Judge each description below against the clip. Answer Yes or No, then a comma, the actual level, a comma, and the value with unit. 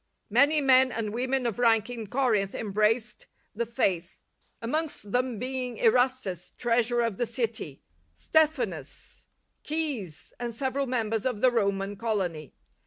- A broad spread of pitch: No, average, 3.6 semitones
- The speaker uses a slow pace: Yes, slow, 130 wpm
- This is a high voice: Yes, high, 235 Hz